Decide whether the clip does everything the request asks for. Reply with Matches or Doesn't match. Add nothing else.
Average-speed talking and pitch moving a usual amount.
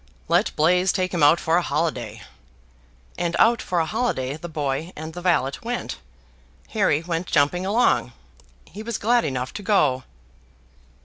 Matches